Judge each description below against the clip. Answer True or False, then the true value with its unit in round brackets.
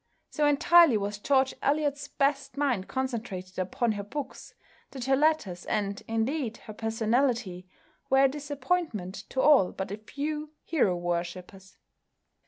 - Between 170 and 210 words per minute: False (135 wpm)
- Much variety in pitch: True (6.2 semitones)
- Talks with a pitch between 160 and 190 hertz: False (245 Hz)